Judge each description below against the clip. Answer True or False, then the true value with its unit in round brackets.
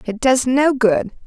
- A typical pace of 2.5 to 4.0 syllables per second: True (3.9 syllables/s)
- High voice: True (245 Hz)